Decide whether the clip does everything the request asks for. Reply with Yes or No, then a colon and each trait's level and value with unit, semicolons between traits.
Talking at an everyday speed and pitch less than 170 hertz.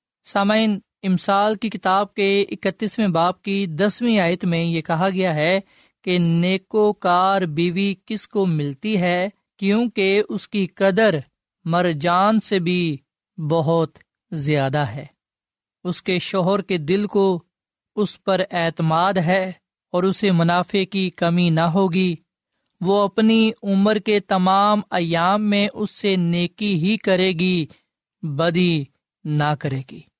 No: average, 135 wpm; medium, 185 Hz